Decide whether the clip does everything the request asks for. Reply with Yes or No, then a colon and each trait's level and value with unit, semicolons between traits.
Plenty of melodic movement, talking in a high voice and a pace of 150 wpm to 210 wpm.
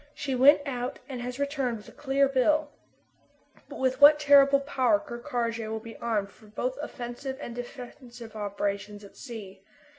No: average, 3.4 semitones; very high, 250 Hz; average, 170 wpm